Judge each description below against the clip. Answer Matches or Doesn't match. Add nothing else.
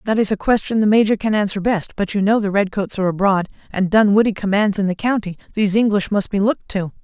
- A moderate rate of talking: Doesn't match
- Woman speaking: Matches